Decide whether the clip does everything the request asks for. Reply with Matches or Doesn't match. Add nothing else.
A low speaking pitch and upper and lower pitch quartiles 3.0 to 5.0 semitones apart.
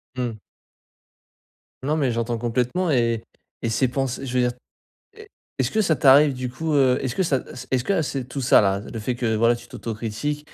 Matches